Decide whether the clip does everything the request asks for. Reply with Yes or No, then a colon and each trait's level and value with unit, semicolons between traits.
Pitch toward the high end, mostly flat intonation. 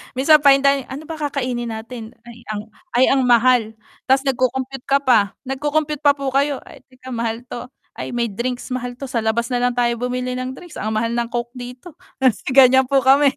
Yes: very high, 255 Hz; narrow, 2.3 semitones